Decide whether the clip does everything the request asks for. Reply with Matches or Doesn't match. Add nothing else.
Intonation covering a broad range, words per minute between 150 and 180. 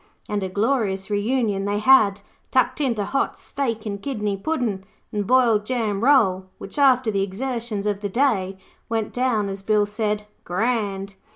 Doesn't match